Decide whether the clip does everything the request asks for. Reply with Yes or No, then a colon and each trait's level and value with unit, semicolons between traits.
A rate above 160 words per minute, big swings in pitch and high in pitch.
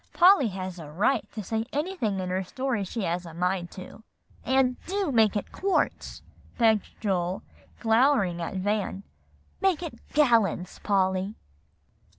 No: average, 145 wpm; wide, 5.9 semitones; high, 210 Hz